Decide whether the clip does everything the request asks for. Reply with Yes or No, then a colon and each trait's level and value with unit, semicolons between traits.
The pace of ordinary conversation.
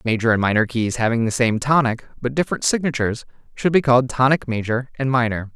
Yes: average, 195 wpm